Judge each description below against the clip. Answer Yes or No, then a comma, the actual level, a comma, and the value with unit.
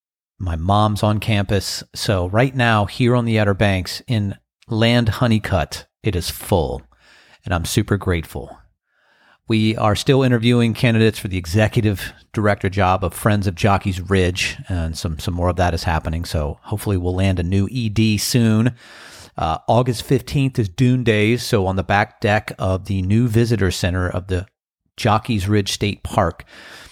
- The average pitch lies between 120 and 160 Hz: No, low, 105 Hz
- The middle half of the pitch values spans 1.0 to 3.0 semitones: No, average, 3.7 semitones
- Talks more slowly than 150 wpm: No, average, 165 wpm